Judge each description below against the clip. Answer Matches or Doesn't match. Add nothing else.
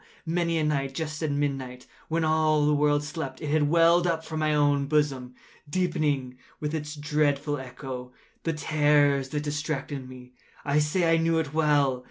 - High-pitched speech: Doesn't match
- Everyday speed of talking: Matches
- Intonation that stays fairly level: Matches